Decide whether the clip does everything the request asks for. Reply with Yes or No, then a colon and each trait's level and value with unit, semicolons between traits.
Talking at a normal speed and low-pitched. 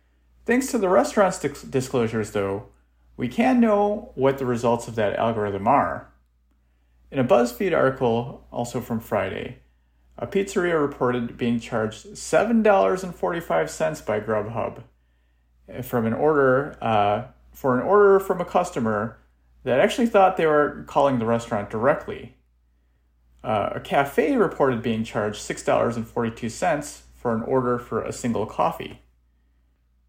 No: slow, 130 wpm; low, 115 Hz